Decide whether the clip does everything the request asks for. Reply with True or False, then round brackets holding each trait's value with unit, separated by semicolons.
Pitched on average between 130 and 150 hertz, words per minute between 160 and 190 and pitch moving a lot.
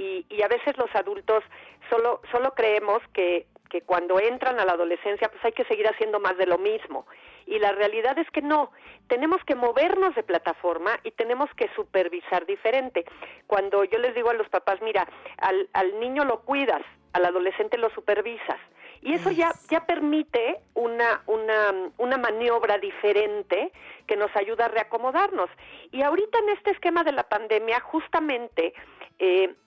False (235 Hz; 170 wpm; 7.9 semitones)